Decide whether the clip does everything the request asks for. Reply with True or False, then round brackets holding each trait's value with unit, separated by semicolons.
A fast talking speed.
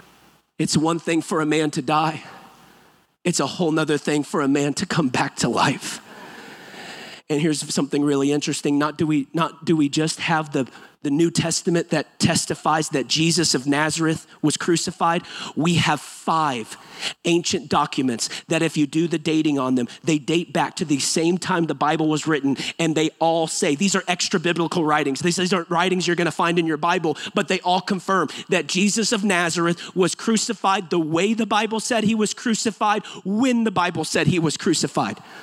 False (195 wpm)